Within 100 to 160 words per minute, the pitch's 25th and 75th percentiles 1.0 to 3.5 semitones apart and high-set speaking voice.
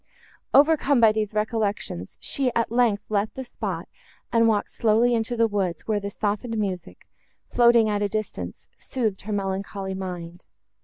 Yes: average, 155 wpm; narrow, 2.6 semitones; high, 215 Hz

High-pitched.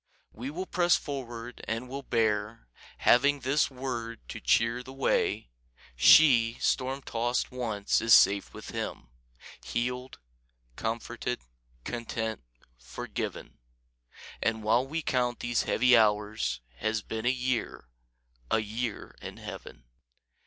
No: low, 120 Hz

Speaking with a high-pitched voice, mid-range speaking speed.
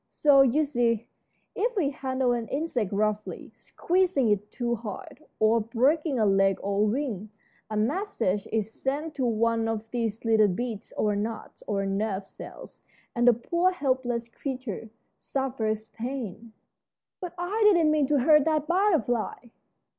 Yes: high, 240 Hz; average, 150 wpm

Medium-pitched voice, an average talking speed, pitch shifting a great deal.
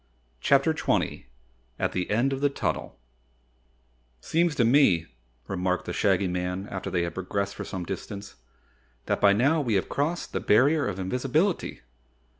No: low, 105 Hz; average, 160 wpm; wide, 7.2 semitones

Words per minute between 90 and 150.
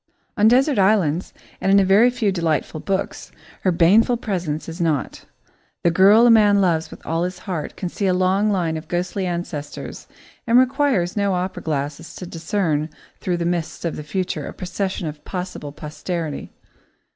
No: average, 175 wpm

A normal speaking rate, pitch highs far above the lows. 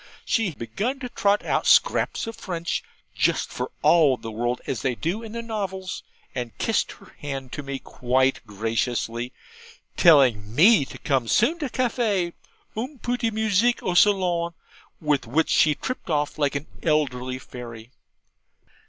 Yes: average, 155 wpm; wide, 8.8 semitones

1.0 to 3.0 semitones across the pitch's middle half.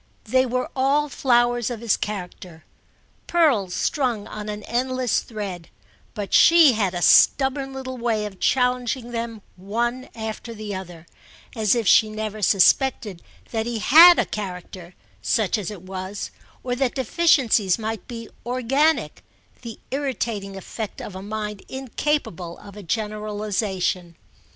No: average, 4.1 semitones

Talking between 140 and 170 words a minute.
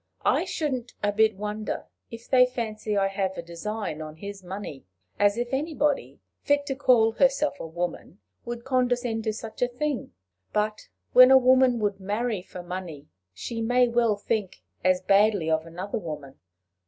Yes: average, 165 wpm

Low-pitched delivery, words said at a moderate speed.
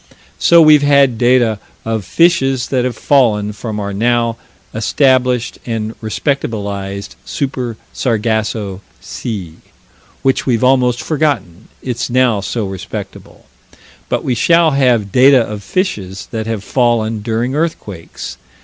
No: low, 120 Hz; slow, 120 wpm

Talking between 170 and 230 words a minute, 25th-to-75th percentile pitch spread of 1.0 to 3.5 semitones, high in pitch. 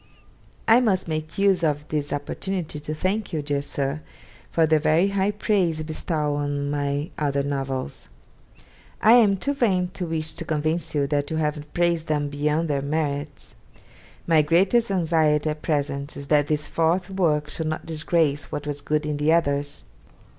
No: average, 175 wpm; average, 2.8 semitones; medium, 155 Hz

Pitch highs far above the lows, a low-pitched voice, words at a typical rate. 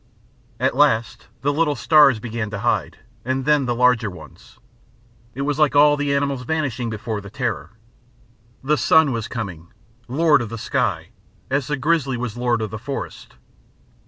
No: average, 4.0 semitones; low, 125 Hz; average, 165 wpm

